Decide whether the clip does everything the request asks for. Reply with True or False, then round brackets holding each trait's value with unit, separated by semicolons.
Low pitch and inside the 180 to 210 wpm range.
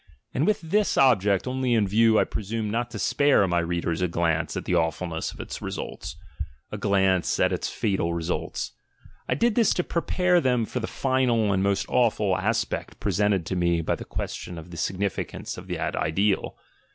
True (100 Hz; 190 wpm)